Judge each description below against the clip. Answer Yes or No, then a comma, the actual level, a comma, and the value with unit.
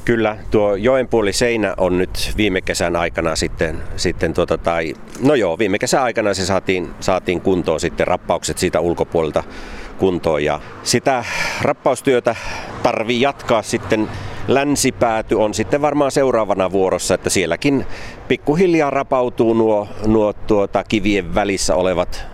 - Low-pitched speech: Yes, low, 105 Hz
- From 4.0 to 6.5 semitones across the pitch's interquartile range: Yes, average, 4.3 semitones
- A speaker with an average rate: Yes, average, 130 wpm